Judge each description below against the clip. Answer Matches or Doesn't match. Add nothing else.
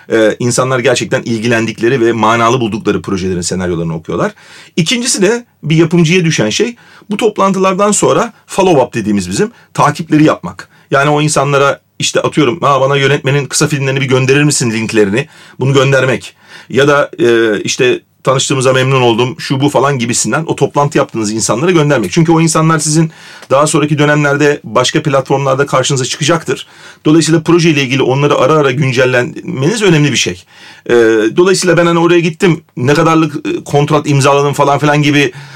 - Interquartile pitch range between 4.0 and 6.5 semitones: Matches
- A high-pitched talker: Doesn't match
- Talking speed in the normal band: Doesn't match